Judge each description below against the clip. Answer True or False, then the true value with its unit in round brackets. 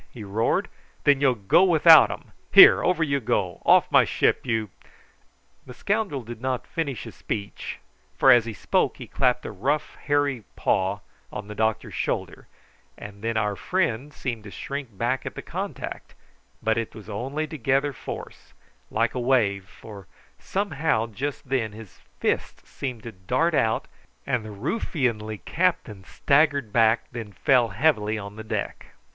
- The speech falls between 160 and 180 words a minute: True (170 wpm)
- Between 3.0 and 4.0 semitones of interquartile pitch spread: False (4.8 semitones)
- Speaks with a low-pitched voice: True (120 Hz)